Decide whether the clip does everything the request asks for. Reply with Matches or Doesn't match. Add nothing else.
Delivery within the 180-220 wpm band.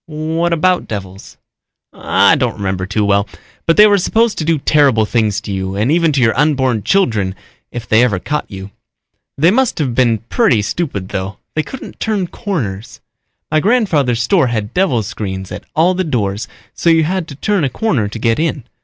Matches